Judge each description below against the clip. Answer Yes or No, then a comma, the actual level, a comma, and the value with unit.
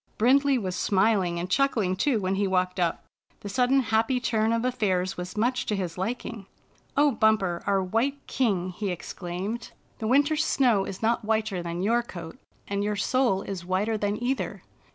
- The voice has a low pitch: No, high, 210 Hz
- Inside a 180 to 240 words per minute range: Yes, average, 190 wpm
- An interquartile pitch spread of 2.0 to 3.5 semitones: No, average, 4.3 semitones